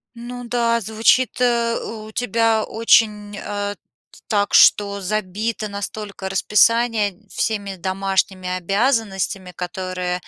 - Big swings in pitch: No, average, 3.0 semitones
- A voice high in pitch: Yes, high, 210 Hz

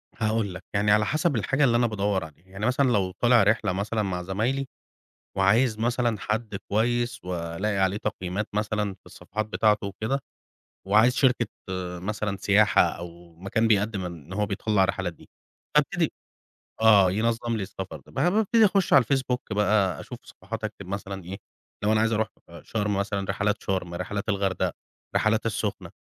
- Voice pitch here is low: Yes, low, 105 Hz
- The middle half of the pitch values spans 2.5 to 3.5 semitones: Yes, average, 2.8 semitones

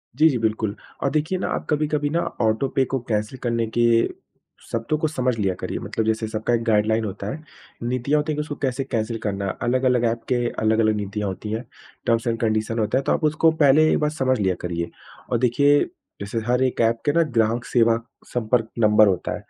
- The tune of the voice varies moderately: Yes, average, 3.8 semitones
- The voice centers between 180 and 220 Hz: No, low, 115 Hz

